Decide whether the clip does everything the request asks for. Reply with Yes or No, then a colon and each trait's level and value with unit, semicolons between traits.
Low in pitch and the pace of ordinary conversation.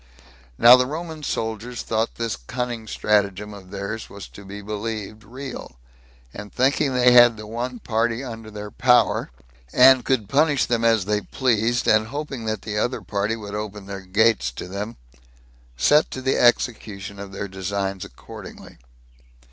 Yes: low, 110 Hz; average, 160 wpm